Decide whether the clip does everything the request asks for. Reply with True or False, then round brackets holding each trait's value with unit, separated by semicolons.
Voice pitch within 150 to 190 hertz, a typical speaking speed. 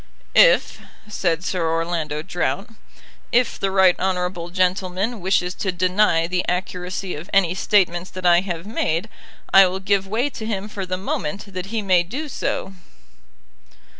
True (185 Hz; 155 wpm)